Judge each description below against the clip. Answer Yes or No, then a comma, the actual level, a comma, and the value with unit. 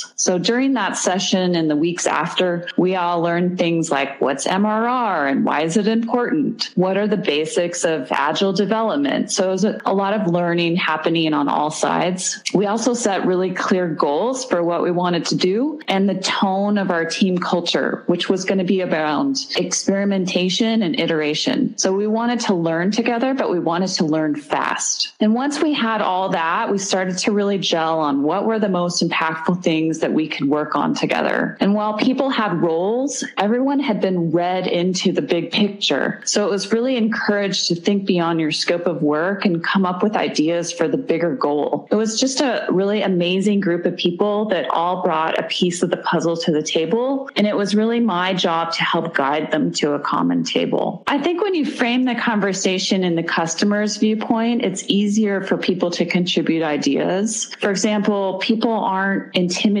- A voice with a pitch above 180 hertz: Yes, high, 190 Hz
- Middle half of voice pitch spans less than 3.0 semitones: No, average, 4.2 semitones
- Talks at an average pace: Yes, average, 195 wpm